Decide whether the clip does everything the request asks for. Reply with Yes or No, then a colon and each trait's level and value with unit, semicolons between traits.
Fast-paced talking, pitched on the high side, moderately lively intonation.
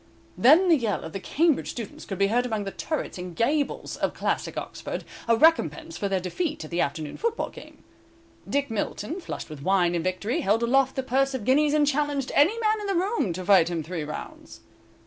No: fast, 210 wpm; high, 245 Hz; wide, 8.2 semitones